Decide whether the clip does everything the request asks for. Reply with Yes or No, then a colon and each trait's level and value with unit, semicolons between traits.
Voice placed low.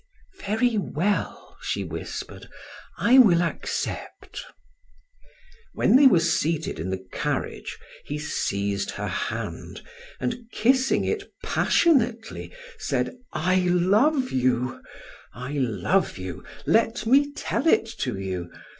No: medium, 180 Hz